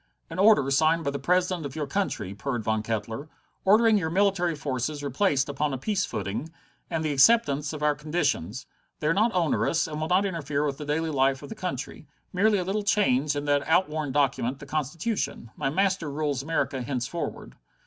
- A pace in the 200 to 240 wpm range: No, average, 190 wpm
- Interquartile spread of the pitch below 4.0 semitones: No, average, 4.6 semitones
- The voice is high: No, medium, 150 Hz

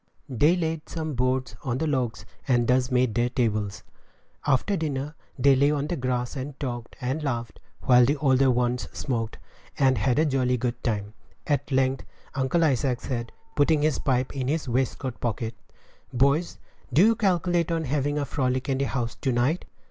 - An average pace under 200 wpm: Yes, average, 175 wpm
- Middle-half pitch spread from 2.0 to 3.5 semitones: Yes, average, 3.0 semitones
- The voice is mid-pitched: No, low, 130 Hz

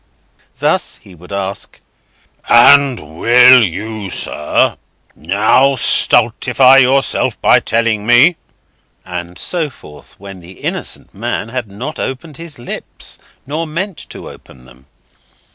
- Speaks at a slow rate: Yes, slow, 115 wpm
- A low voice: Yes, low, 115 Hz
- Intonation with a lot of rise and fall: Yes, wide, 6.2 semitones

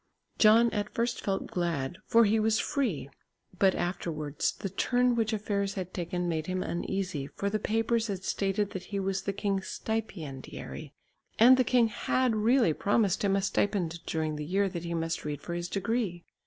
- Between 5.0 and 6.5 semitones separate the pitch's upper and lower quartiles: No, average, 4.3 semitones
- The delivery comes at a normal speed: Yes, average, 180 wpm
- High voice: Yes, high, 195 Hz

